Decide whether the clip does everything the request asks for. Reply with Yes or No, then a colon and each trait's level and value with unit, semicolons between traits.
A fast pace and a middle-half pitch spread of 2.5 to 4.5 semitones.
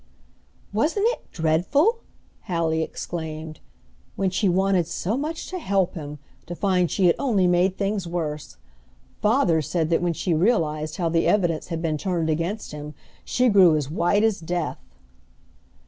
No: average, 155 wpm; average, 3.9 semitones